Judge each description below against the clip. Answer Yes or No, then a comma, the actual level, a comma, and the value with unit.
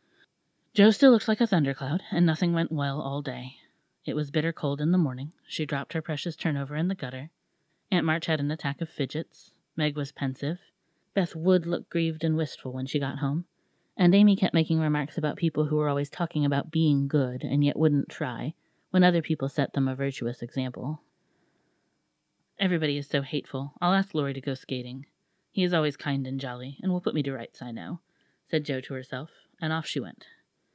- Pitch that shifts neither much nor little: Yes, average, 3.4 semitones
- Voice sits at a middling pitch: Yes, medium, 150 Hz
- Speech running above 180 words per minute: Yes, fast, 205 wpm